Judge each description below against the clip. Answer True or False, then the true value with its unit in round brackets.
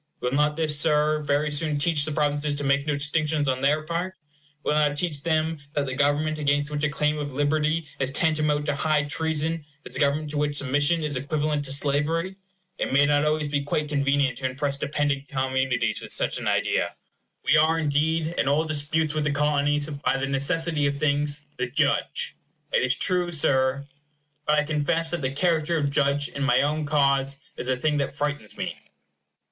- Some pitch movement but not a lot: False (1.5 semitones)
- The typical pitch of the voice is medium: True (145 Hz)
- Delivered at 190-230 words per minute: True (200 wpm)